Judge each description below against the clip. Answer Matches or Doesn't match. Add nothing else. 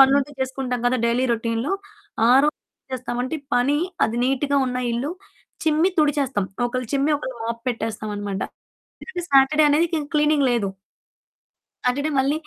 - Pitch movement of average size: Matches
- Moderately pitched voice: Doesn't match